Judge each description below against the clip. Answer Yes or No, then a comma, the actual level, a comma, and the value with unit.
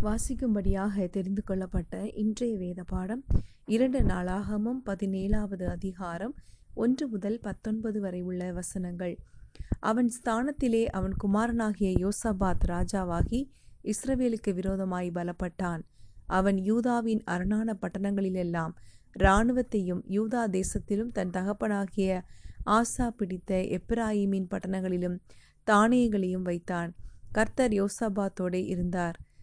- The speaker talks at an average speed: Yes, average, 90 wpm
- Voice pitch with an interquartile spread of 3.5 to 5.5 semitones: No, average, 3.1 semitones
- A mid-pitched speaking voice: No, high, 200 Hz